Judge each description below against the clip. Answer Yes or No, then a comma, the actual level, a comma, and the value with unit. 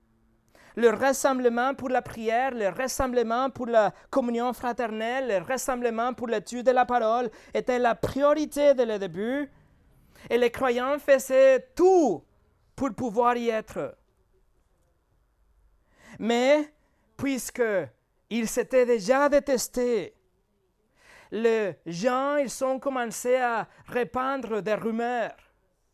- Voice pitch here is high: Yes, high, 245 Hz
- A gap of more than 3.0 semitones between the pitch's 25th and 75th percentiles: No, narrow, 2.6 semitones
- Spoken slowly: Yes, slow, 110 wpm